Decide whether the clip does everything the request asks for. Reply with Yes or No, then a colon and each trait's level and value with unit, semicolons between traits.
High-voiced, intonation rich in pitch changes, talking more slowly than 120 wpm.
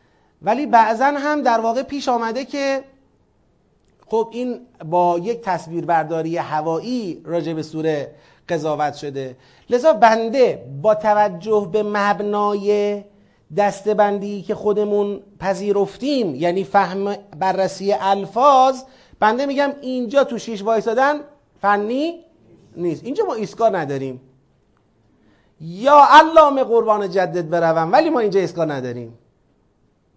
Yes: high, 205 Hz; wide, 6.2 semitones; average, 110 wpm